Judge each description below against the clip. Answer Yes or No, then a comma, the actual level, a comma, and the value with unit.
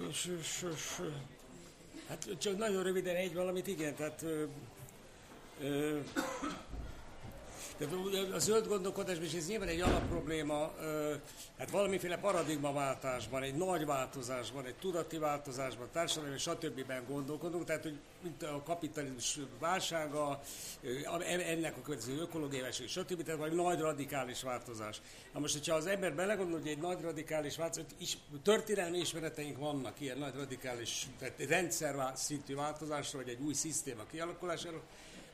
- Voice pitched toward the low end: No, medium, 155 Hz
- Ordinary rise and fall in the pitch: Yes, average, 3.6 semitones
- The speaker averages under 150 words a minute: Yes, average, 125 wpm